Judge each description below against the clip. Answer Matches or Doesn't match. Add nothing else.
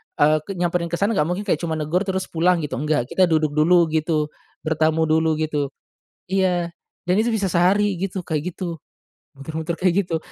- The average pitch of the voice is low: Doesn't match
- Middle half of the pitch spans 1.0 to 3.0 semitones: Matches